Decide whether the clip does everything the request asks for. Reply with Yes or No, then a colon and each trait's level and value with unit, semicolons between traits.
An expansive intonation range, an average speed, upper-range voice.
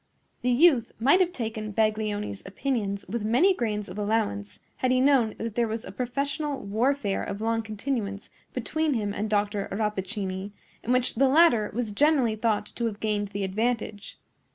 No: average, 3.5 semitones; average, 170 wpm; high, 220 Hz